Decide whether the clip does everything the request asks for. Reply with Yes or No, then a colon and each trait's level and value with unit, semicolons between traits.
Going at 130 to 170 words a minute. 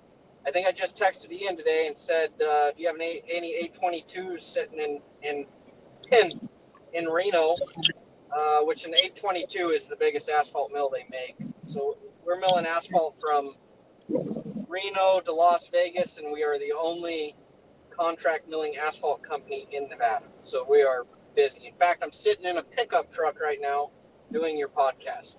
Yes: average, 165 wpm